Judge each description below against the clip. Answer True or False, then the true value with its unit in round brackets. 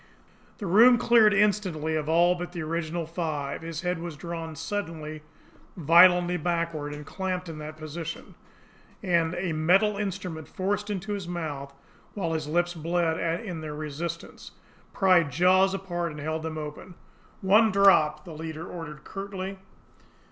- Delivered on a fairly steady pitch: False (3.0 semitones)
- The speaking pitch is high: False (170 Hz)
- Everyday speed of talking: True (150 wpm)